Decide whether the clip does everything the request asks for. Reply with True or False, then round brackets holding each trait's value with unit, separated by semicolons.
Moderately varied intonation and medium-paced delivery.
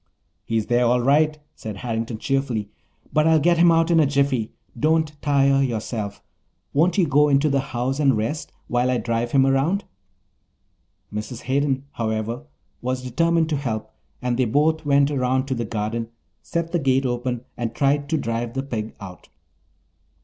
True (3.9 semitones; 170 wpm)